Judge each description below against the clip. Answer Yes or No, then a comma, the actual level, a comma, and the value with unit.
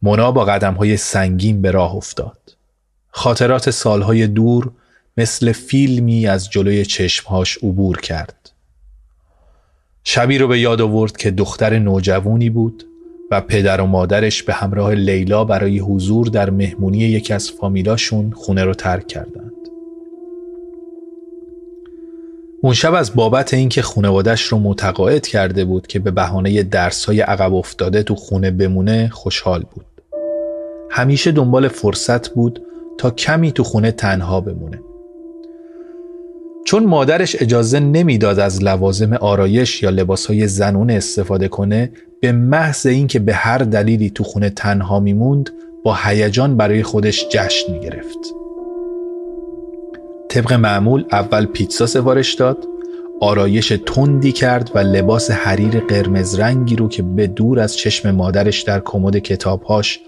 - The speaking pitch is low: Yes, low, 110 Hz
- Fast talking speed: No, average, 130 wpm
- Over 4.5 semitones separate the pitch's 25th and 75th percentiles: Yes, average, 5.3 semitones